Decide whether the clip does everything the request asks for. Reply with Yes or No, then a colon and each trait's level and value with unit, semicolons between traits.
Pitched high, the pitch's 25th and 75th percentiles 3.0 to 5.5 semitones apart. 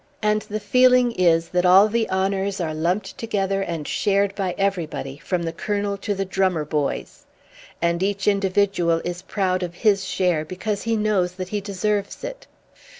No: high, 195 Hz; narrow, 2.5 semitones